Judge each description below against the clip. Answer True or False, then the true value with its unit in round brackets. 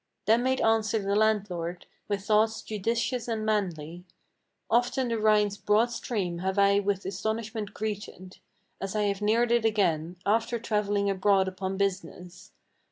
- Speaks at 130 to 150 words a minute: True (145 wpm)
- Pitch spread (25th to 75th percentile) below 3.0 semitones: True (2.4 semitones)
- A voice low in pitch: False (210 Hz)